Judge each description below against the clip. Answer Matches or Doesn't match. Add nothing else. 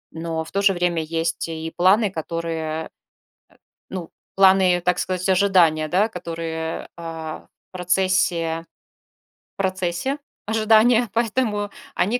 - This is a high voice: Doesn't match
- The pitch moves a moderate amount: Matches